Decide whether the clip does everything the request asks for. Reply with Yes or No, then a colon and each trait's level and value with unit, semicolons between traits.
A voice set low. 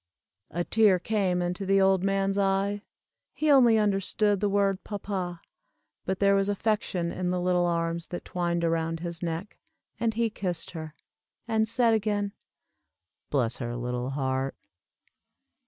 No: high, 190 Hz